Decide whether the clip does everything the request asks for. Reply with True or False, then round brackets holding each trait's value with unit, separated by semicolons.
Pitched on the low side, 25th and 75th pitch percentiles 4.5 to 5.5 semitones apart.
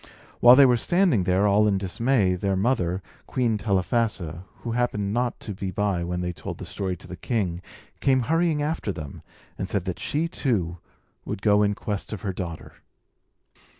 True (100 Hz; 4.8 semitones)